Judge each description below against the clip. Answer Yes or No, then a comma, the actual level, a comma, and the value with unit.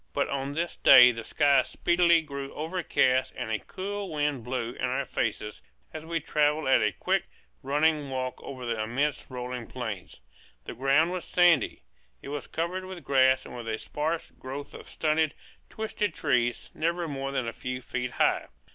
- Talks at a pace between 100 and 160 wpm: No, average, 175 wpm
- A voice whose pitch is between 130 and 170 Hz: Yes, medium, 140 Hz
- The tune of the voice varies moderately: Yes, average, 4.2 semitones